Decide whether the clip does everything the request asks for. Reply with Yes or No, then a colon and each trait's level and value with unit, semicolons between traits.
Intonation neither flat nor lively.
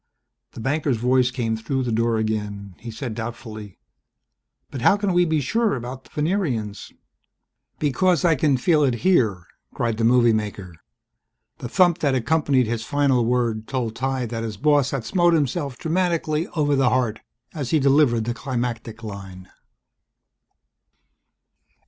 Yes: average, 4.7 semitones